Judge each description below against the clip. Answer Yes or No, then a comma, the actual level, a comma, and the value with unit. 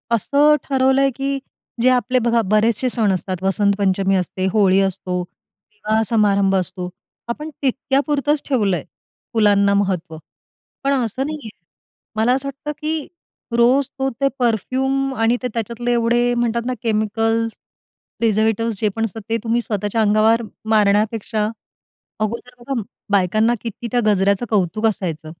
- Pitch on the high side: Yes, high, 225 Hz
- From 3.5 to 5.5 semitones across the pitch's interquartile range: Yes, average, 3.8 semitones